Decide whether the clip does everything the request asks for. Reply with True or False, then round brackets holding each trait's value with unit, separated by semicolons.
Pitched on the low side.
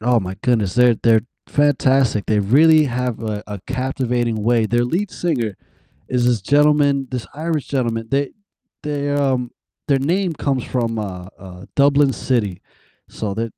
True (125 Hz)